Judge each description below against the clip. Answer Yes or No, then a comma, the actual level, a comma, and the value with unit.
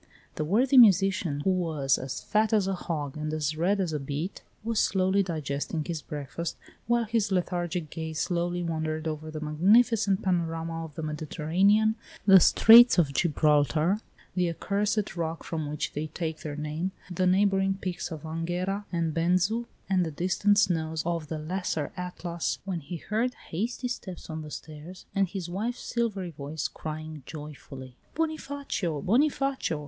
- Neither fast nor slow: Yes, average, 160 wpm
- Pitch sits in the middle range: Yes, medium, 175 Hz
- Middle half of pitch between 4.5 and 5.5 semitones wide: No, average, 4.0 semitones